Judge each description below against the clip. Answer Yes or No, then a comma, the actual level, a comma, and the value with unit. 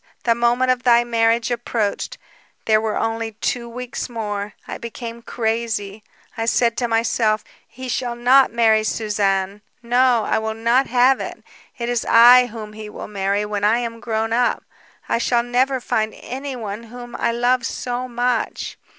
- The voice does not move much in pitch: Yes, narrow, 1.9 semitones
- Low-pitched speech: No, high, 235 Hz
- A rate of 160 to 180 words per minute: Yes, average, 165 wpm